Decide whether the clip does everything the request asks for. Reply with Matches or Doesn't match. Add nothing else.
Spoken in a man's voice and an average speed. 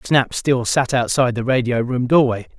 Matches